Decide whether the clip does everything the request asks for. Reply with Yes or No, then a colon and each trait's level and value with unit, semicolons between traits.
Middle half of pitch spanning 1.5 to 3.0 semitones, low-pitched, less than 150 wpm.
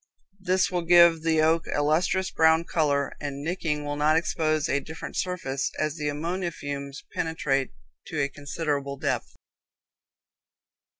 No: average, 2.7 semitones; medium, 155 Hz; average, 140 wpm